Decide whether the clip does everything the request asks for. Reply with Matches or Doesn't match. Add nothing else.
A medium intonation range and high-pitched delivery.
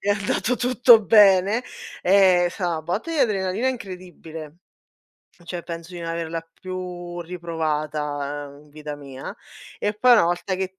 Doesn't match